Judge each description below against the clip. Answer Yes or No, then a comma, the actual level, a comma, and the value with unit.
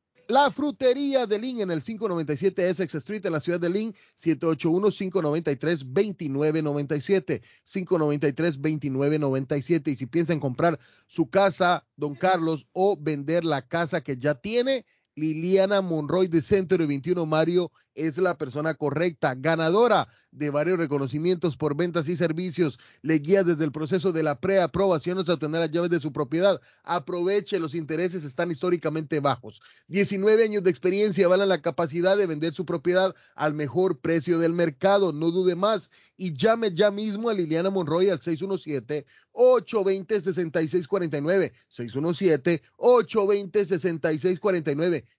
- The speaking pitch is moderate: Yes, medium, 175 Hz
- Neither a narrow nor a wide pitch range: Yes, average, 3.5 semitones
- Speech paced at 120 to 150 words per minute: Yes, average, 140 wpm